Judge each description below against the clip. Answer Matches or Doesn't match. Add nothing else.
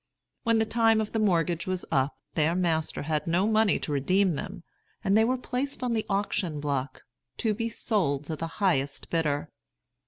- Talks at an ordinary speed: Matches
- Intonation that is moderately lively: Doesn't match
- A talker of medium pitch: Matches